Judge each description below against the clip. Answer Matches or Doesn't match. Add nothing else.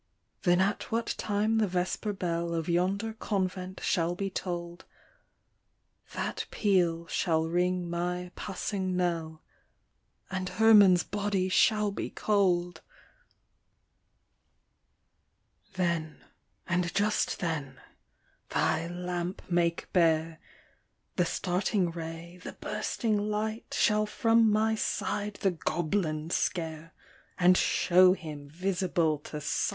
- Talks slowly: Matches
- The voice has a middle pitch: Matches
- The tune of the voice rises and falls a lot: Doesn't match